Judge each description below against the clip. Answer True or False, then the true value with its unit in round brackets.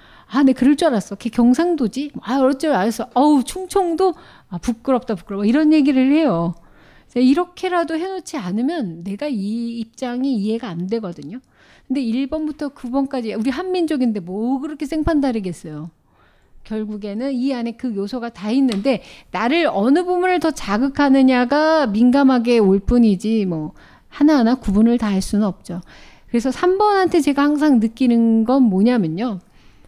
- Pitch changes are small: False (5.3 semitones)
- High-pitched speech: True (250 Hz)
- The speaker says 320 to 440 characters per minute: True (325 characters per minute)